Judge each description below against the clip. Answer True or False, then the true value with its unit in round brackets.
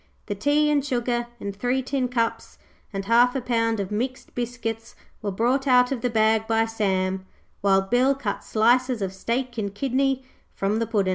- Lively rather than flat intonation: False (3.4 semitones)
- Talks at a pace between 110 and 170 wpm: False (185 wpm)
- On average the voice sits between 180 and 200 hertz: False (230 Hz)